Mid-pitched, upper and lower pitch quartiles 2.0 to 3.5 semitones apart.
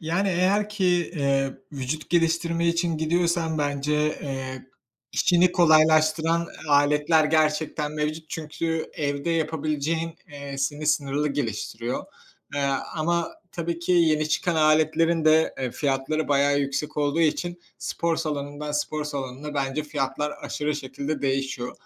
Yes: medium, 155 Hz; narrow, 2.5 semitones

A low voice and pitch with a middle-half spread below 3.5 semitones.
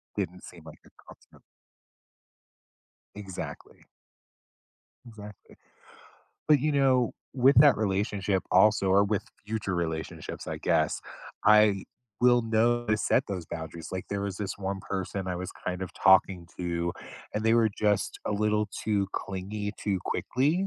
Yes: low, 100 Hz; average, 2.7 semitones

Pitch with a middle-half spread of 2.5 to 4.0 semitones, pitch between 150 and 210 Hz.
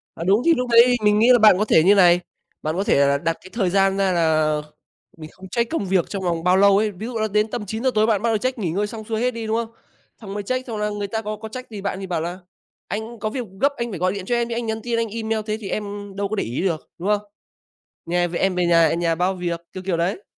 Yes: average, 3.7 semitones; high, 205 Hz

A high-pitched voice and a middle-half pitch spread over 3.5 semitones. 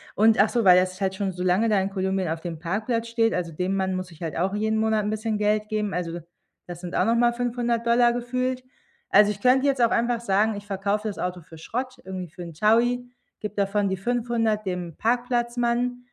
Yes: high, 210 Hz; average, 4.1 semitones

